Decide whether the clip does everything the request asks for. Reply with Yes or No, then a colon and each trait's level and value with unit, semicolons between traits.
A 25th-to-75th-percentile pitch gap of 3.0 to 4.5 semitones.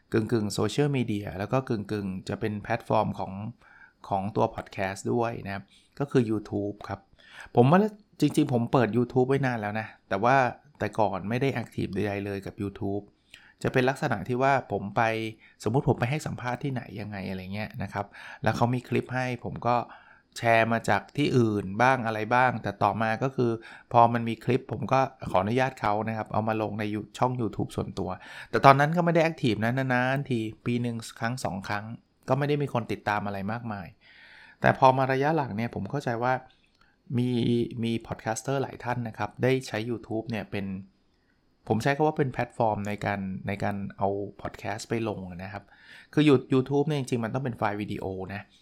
Yes: average, 4.0 semitones